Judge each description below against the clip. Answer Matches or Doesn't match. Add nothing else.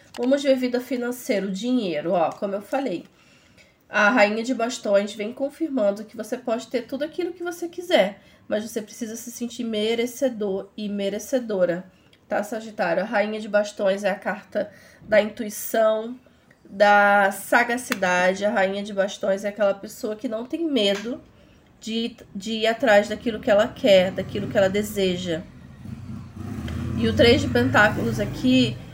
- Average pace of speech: Matches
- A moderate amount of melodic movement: Matches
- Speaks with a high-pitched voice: Matches